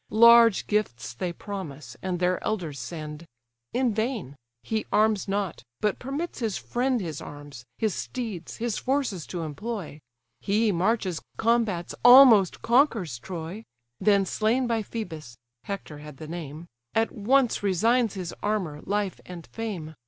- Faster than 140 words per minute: No, slow, 135 wpm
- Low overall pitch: No, high, 200 Hz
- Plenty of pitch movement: Yes, wide, 5.7 semitones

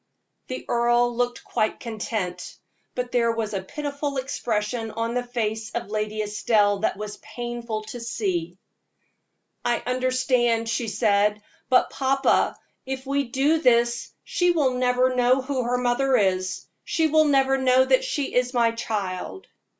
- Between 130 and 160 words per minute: Yes, average, 150 wpm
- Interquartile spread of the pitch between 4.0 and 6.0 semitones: No, average, 3.1 semitones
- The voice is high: Yes, high, 240 Hz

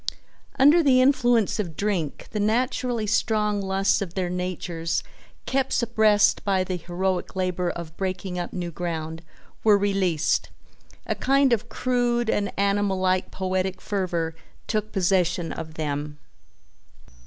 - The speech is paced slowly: Yes, slow, 130 wpm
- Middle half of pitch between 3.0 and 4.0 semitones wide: Yes, average, 3.6 semitones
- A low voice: No, high, 190 Hz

